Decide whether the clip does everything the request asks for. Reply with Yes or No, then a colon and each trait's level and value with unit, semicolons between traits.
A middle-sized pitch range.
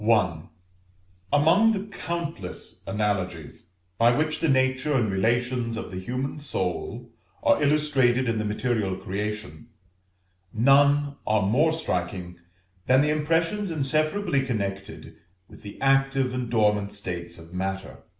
No: wide, 6.5 semitones